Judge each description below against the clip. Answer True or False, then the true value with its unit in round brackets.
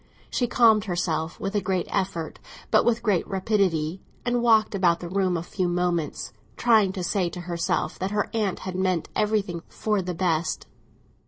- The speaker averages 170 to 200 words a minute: True (175 wpm)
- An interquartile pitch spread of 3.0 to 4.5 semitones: True (3.3 semitones)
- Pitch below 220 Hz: True (185 Hz)